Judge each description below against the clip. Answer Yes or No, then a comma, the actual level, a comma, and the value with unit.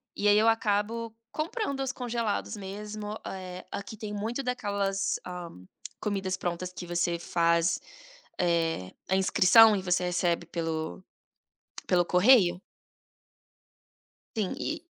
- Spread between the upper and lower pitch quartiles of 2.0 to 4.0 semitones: Yes, average, 3.7 semitones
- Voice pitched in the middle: No, high, 195 Hz